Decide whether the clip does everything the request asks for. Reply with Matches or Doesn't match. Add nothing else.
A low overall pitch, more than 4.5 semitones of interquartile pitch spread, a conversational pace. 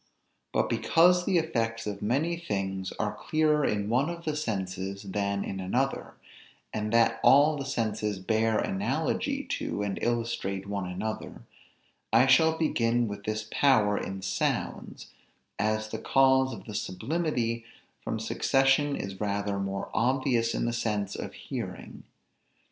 Matches